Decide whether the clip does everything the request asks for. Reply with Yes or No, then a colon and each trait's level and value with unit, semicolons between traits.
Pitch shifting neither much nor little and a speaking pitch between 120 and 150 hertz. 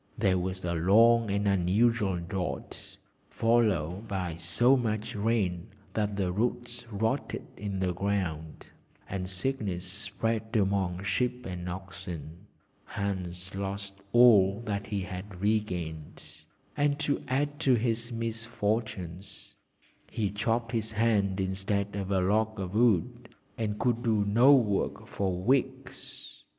No: average, 3.5 semitones; low, 100 Hz